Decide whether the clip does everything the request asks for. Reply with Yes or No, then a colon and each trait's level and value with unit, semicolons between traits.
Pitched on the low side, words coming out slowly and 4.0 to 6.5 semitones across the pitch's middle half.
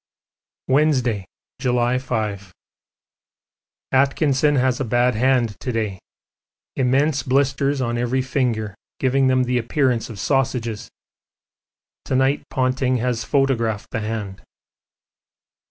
No: low, 125 Hz; slow, 105 wpm; average, 2.8 semitones